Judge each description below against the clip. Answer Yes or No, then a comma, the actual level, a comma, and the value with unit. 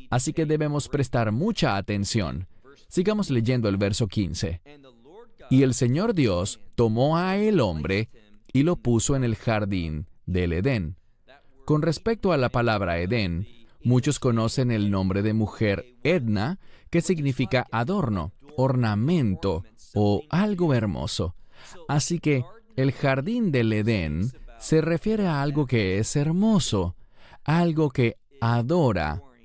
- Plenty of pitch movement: Yes, wide, 6.1 semitones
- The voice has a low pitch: Yes, low, 120 Hz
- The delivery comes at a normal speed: No, slow, 130 wpm